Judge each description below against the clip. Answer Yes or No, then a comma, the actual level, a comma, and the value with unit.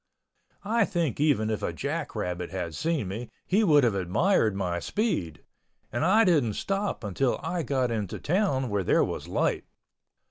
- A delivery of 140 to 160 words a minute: No, average, 170 wpm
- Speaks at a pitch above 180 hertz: No, low, 130 Hz